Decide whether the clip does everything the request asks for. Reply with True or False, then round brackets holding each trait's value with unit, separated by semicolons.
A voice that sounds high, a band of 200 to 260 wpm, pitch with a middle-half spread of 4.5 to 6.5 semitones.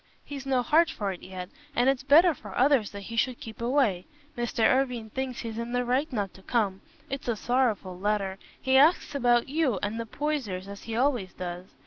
True (240 Hz; 205 wpm; 4.8 semitones)